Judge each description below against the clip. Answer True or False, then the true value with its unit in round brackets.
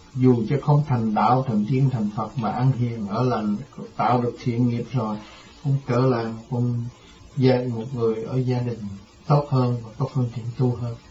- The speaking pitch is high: False (120 Hz)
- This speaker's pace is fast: False (195 wpm)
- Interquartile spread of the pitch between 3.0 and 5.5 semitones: False (2.4 semitones)